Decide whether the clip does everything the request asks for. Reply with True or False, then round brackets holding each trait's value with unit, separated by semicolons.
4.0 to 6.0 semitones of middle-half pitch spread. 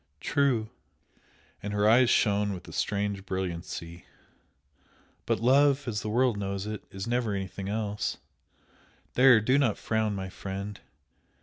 False (3.3 semitones)